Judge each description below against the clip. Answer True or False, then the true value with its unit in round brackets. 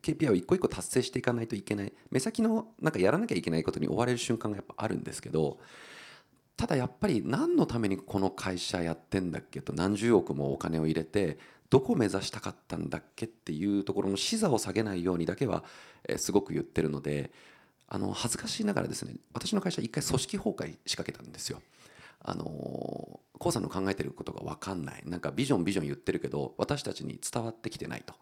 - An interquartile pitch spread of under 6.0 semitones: True (5.3 semitones)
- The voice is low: True (95 Hz)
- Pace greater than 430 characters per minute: True (440 characters per minute)